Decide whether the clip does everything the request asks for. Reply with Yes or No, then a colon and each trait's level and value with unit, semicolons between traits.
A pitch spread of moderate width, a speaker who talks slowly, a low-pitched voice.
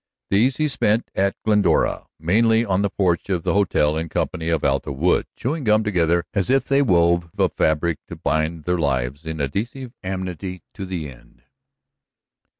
No: average, 4.6 semitones; average, 170 wpm; very low, 90 Hz